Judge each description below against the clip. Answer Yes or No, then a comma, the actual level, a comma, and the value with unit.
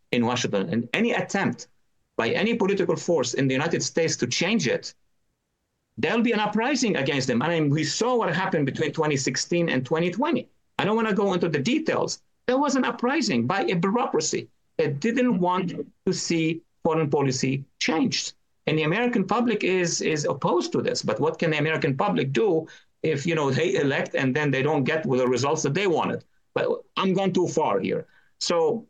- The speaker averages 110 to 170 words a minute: No, average, 195 wpm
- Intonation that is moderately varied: No, wide, 6.6 semitones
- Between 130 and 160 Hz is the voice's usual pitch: No, medium, 175 Hz